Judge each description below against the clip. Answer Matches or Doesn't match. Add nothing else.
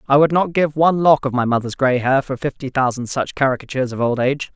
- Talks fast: Matches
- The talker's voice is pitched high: Doesn't match